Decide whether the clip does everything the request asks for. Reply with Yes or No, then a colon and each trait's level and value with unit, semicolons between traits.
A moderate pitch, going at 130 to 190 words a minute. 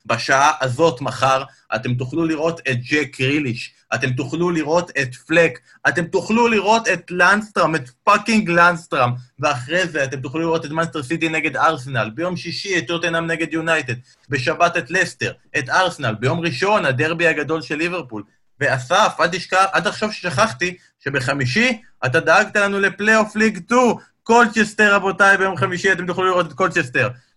Yes: medium, 165 Hz; fast, 150 wpm